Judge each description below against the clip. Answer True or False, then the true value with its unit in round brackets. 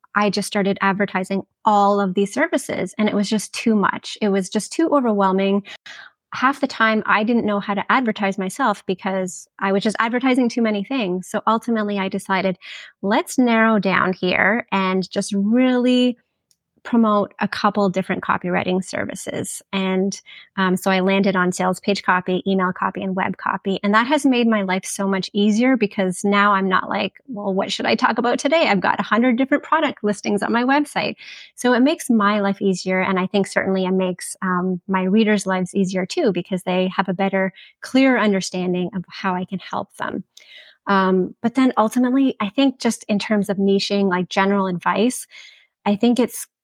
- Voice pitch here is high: True (200 Hz)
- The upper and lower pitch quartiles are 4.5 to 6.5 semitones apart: False (3.1 semitones)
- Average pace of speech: True (190 wpm)